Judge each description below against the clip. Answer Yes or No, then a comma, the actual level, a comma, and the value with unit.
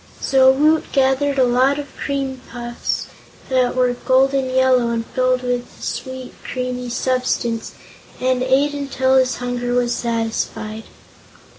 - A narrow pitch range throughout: Yes, narrow, 1.4 semitones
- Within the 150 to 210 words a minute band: No, average, 140 wpm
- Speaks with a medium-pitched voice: No, very high, 255 Hz